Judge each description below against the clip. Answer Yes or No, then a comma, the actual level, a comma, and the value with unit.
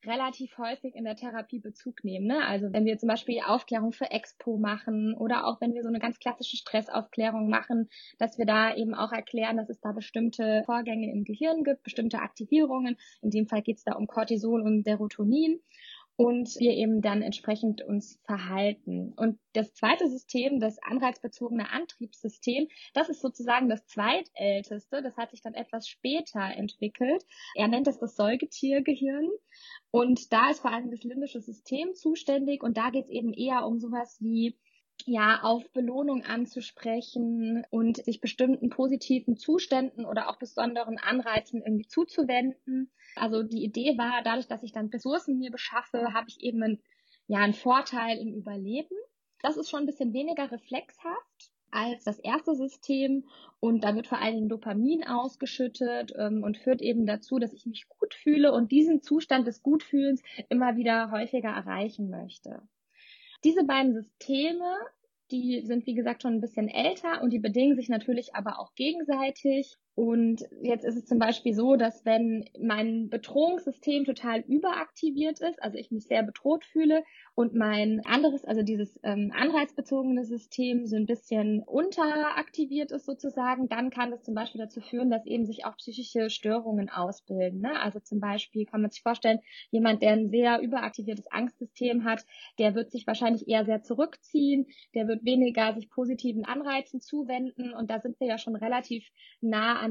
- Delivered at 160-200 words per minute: Yes, average, 170 wpm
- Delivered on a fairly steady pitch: No, average, 3.3 semitones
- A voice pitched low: No, high, 240 Hz